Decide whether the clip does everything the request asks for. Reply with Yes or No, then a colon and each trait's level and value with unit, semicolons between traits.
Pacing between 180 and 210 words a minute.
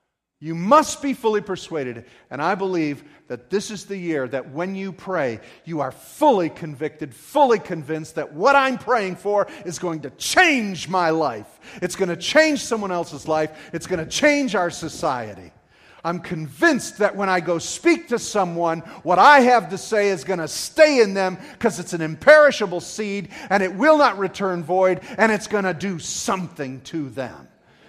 Yes: average, 185 wpm